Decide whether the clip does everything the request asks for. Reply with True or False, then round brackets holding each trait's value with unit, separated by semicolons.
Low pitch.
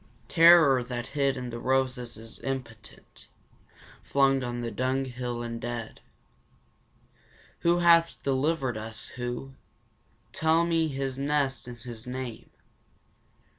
True (130 Hz)